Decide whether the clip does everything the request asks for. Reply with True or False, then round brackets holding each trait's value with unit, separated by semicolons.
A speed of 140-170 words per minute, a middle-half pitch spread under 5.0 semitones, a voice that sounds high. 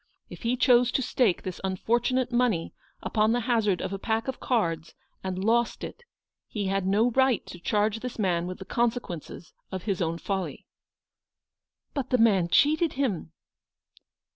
True (165 wpm; 4.6 semitones; 220 Hz)